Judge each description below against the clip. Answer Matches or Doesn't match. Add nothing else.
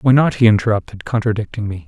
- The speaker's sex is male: Matches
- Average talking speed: Matches